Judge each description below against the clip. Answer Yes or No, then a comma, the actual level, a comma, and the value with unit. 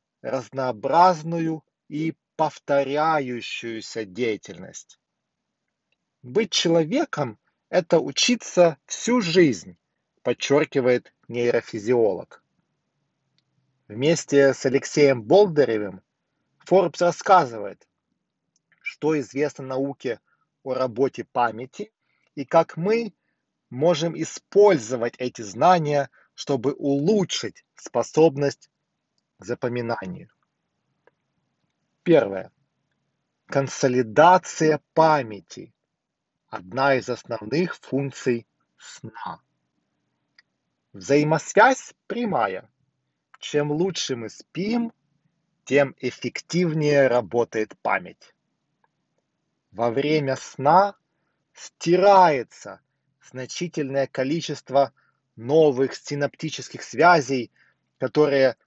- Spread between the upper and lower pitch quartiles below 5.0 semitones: Yes, average, 4.3 semitones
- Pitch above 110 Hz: Yes, medium, 140 Hz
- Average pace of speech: No, slow, 65 wpm